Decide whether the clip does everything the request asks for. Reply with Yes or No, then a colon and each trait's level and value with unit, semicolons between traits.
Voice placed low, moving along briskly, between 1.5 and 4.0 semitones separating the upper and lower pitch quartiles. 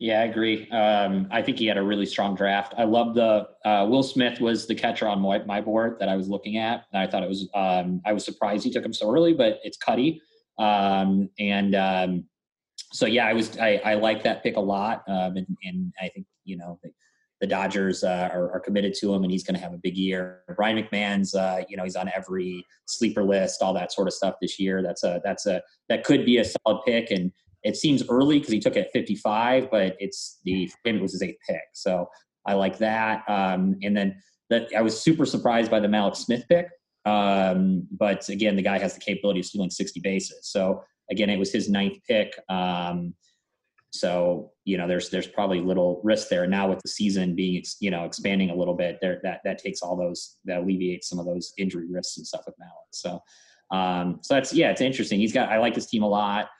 Yes: low, 100 Hz; fast, 235 wpm; average, 2.9 semitones